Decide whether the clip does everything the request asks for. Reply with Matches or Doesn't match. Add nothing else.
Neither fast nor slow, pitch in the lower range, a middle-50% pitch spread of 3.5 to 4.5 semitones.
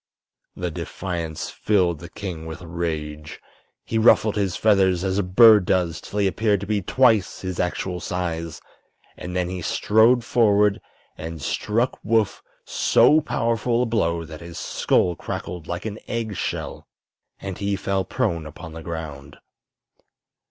Matches